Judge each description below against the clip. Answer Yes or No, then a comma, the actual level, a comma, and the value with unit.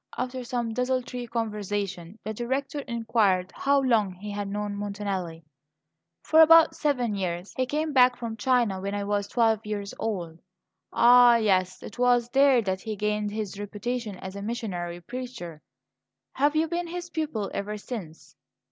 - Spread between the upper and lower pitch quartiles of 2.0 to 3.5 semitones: No, average, 3.9 semitones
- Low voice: No, high, 220 Hz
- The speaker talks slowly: No, average, 155 wpm